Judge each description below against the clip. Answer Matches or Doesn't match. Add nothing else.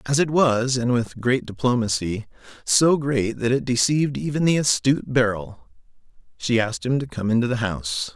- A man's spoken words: Matches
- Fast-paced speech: Doesn't match